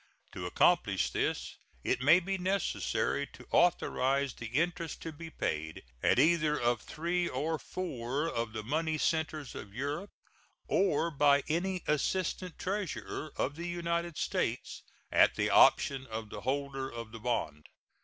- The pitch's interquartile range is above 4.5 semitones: Yes, average, 5.2 semitones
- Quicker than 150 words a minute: No, average, 145 wpm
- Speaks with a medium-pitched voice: Yes, medium, 150 Hz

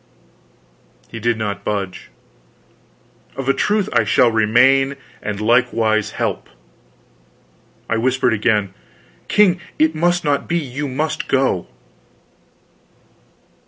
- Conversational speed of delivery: No, slow, 105 wpm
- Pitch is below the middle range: Yes, low, 125 Hz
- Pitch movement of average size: Yes, average, 4.8 semitones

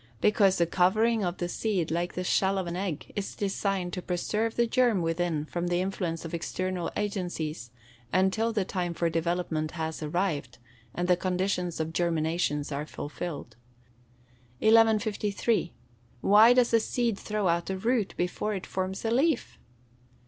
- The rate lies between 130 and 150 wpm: No, average, 160 wpm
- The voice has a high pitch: No, medium, 180 Hz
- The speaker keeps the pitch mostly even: No, average, 3.5 semitones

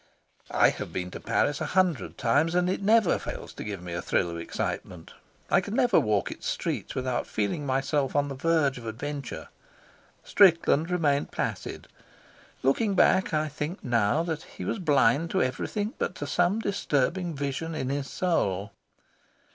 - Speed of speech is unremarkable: Yes, average, 170 wpm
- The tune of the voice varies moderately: No, wide, 5.7 semitones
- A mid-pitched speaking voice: Yes, medium, 145 Hz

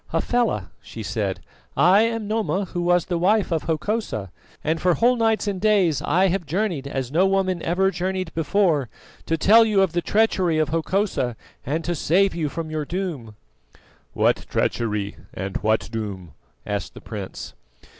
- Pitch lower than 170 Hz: No, medium, 175 Hz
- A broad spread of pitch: Yes, wide, 5.8 semitones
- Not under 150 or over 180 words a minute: Yes, average, 165 wpm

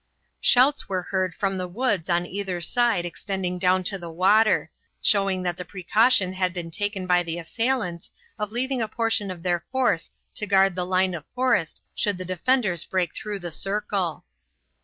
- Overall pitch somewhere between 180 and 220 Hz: Yes, high, 190 Hz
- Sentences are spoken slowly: No, average, 180 wpm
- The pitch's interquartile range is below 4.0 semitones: Yes, average, 3.0 semitones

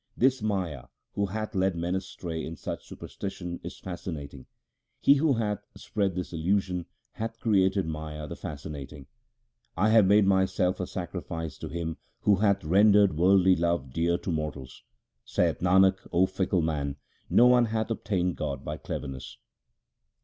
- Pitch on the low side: Yes, very low, 90 Hz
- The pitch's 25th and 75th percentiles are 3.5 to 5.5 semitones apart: Yes, average, 3.8 semitones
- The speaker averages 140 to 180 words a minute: Yes, average, 150 wpm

